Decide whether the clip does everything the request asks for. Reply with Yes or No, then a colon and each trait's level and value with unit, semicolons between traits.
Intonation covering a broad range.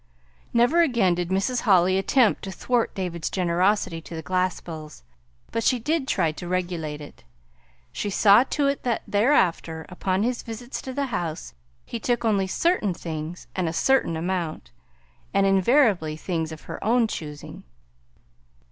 Yes: wide, 5.8 semitones